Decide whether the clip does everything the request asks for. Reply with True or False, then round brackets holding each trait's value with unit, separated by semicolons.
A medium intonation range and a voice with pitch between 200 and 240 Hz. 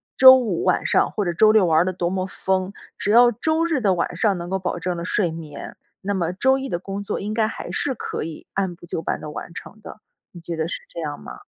False (4.0 semitones; 190 Hz)